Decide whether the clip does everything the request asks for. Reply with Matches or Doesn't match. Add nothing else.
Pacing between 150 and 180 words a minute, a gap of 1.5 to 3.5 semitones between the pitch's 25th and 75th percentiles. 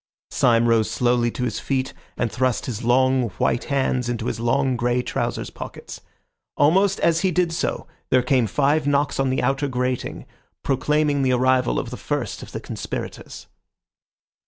Matches